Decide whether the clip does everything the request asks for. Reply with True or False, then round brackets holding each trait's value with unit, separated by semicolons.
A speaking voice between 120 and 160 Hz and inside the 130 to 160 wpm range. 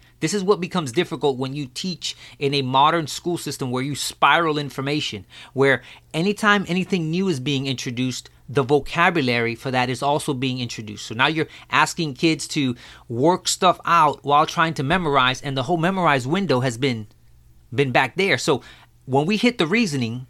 False (140 Hz; 180 wpm)